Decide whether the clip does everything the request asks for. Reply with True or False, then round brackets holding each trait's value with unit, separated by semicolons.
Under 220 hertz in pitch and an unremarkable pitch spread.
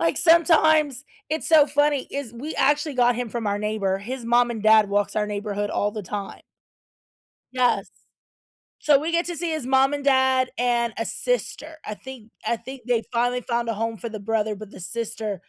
False (240 Hz; 4.6 semitones)